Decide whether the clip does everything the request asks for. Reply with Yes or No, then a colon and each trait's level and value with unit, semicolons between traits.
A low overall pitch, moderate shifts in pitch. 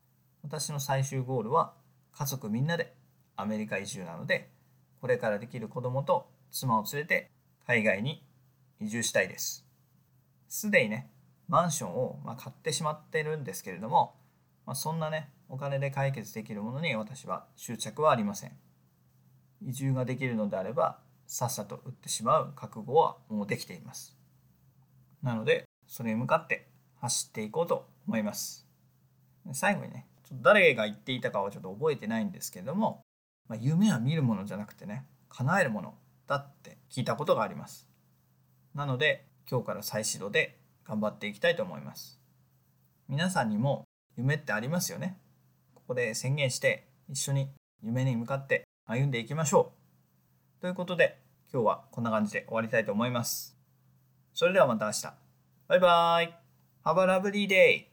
No: low, 130 Hz; wide, 6.6 semitones